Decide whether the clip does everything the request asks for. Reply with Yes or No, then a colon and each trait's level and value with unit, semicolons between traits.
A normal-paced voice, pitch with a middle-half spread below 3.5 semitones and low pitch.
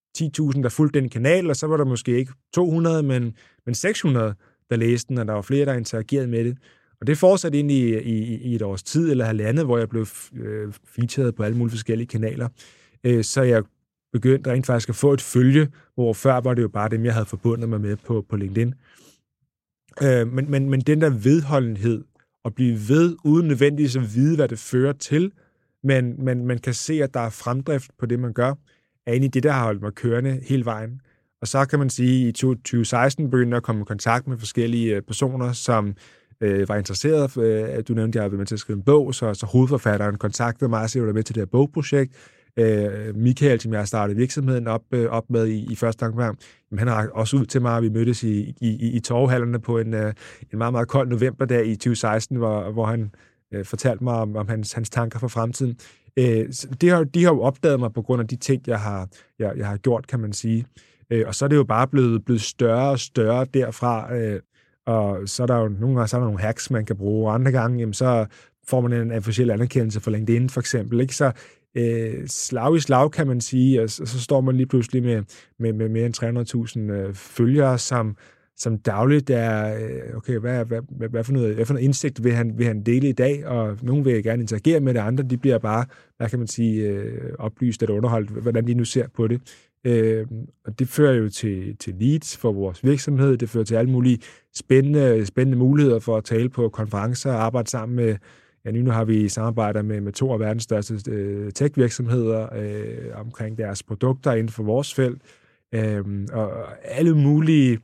Yes: average, 215 wpm; average, 2.9 semitones; low, 120 Hz